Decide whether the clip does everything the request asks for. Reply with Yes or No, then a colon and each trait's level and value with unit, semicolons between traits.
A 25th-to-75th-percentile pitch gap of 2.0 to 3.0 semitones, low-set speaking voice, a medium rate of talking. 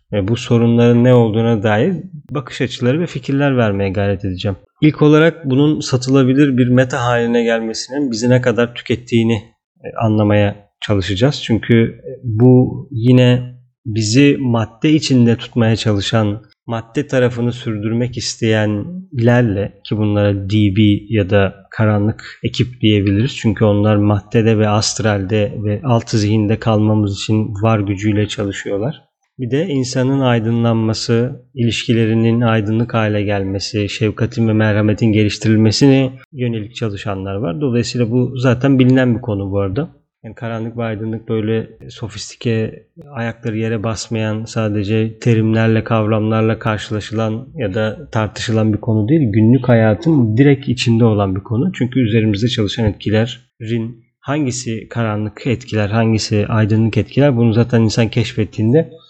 Yes: narrow, 2.6 semitones; low, 115 Hz; average, 125 wpm